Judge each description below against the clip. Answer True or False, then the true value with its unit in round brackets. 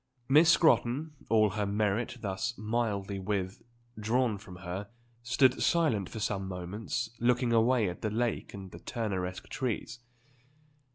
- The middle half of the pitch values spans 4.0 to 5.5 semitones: False (3.5 semitones)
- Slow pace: True (130 wpm)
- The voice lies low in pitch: True (110 Hz)